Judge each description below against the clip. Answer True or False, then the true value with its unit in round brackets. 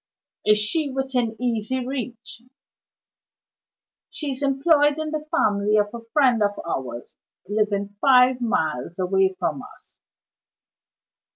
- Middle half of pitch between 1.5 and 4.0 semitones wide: False (4.8 semitones)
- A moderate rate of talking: False (115 wpm)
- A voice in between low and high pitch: False (235 Hz)